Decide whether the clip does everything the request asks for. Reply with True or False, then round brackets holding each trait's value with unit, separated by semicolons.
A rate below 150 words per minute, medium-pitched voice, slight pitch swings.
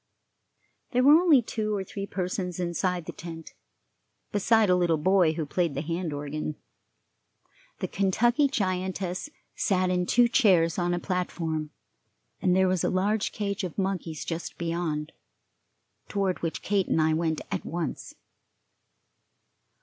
False (140 wpm; 180 Hz; 3.1 semitones)